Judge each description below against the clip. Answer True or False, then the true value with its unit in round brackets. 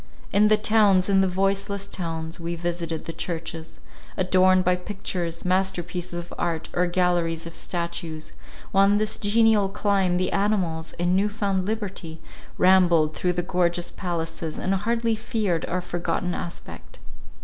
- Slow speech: False (150 wpm)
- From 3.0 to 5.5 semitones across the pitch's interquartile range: False (2.6 semitones)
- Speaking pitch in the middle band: True (180 Hz)